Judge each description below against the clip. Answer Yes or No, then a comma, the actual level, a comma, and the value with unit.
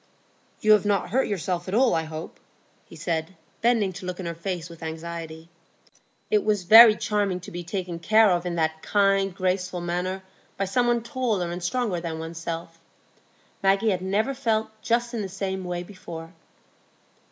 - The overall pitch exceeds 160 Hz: Yes, medium, 185 Hz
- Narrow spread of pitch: No, average, 3.8 semitones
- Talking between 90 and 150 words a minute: No, average, 180 wpm